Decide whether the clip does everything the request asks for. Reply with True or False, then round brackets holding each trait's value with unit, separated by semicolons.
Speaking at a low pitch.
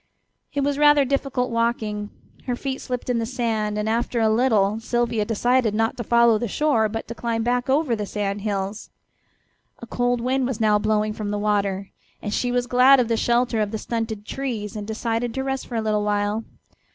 False (230 Hz)